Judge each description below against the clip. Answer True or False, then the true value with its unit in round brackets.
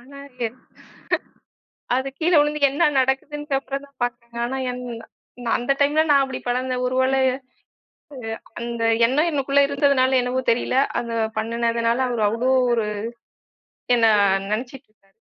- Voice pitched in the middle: False (255 Hz)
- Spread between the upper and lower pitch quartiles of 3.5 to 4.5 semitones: False (2.9 semitones)